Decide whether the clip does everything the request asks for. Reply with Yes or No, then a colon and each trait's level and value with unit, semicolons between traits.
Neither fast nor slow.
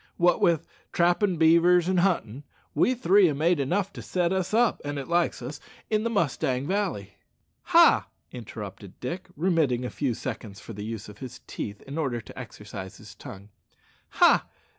Yes: average, 180 wpm